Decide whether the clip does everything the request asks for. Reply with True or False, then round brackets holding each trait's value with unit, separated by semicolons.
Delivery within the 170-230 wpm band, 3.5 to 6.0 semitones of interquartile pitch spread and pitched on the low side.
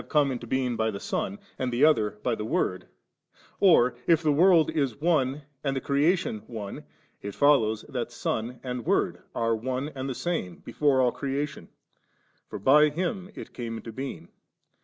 True (180 wpm; 4.5 semitones; 130 Hz)